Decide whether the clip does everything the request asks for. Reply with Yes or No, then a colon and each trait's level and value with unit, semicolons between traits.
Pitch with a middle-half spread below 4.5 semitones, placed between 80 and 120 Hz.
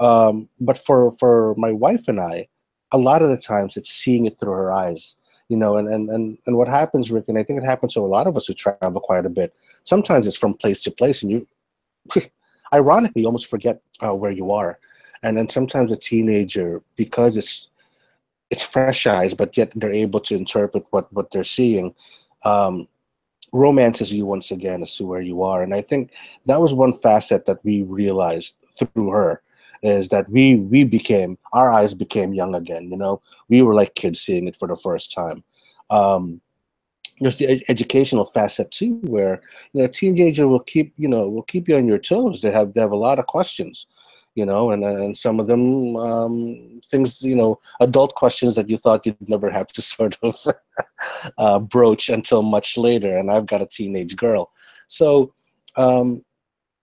Yes: average, 4.0 semitones; low, 115 Hz